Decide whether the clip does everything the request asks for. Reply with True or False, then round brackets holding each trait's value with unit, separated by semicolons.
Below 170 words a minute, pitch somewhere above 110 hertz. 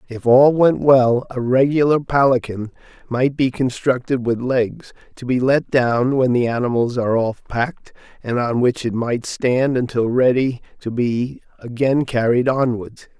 True (160 wpm; 125 Hz)